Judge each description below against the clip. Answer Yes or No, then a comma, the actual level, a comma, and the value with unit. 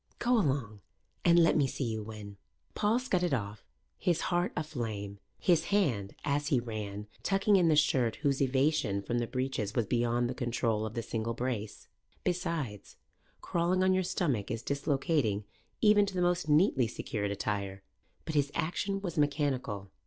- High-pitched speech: No, low, 135 Hz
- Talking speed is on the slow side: No, average, 165 wpm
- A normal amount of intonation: No, wide, 7.6 semitones